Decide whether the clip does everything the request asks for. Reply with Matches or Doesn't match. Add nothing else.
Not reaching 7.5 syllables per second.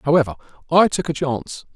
Matches